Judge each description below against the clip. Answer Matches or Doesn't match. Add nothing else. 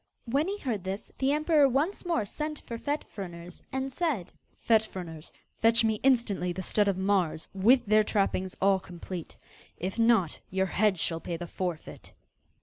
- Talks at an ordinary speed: Matches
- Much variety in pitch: Matches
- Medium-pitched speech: Doesn't match